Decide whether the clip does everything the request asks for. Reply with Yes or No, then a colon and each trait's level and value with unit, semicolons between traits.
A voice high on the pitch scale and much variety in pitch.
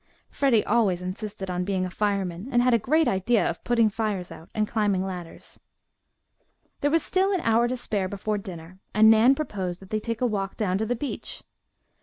No: high, 210 Hz; average, 4.0 semitones